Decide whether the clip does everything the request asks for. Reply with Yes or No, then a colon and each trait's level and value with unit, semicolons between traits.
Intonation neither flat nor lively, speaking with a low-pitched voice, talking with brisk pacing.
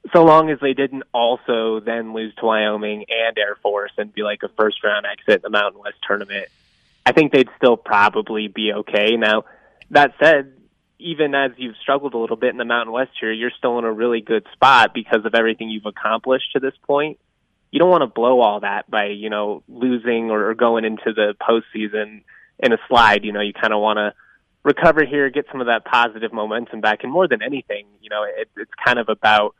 Yes: average, 3.7 semitones; low, 115 Hz; fast, 220 wpm